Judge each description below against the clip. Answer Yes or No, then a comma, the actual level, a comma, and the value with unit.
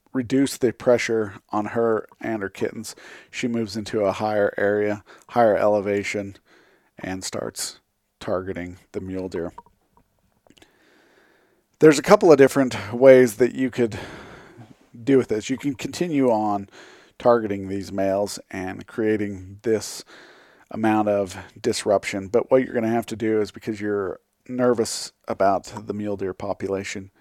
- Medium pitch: No, low, 105 Hz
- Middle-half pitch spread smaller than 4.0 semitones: Yes, average, 3.3 semitones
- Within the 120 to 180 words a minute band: Yes, average, 140 wpm